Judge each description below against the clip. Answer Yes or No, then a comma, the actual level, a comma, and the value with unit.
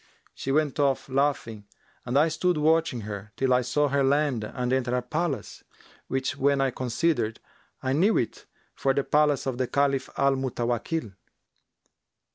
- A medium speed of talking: Yes, average, 160 wpm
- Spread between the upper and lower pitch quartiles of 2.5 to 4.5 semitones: Yes, average, 2.9 semitones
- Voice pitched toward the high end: No, low, 135 Hz